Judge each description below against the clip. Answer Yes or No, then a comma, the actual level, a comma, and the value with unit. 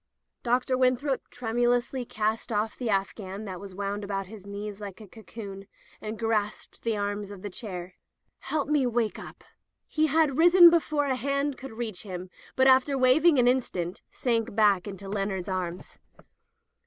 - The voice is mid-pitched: No, high, 220 Hz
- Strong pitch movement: No, average, 4.6 semitones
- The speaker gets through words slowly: No, average, 160 wpm